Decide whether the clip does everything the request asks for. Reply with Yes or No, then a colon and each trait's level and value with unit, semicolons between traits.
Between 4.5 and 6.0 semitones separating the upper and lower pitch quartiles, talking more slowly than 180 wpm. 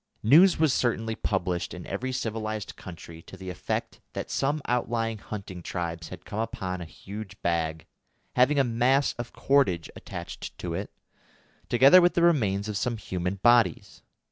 Yes: average, 5.3 semitones; average, 160 wpm